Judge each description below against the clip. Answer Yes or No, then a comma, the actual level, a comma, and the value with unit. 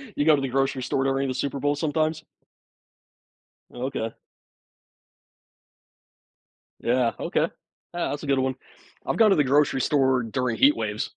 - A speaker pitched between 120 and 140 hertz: Yes, low, 135 Hz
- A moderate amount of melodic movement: No, narrow, 2.3 semitones